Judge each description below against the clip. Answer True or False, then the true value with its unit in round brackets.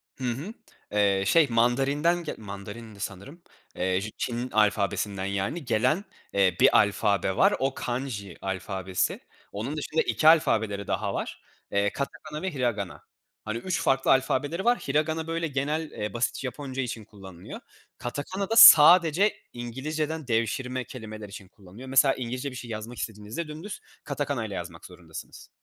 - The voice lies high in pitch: False (120 Hz)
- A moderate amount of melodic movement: False (6.5 semitones)